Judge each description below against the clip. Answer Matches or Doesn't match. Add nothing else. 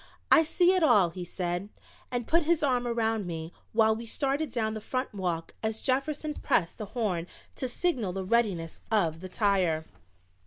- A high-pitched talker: Matches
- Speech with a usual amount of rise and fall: Doesn't match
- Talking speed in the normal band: Matches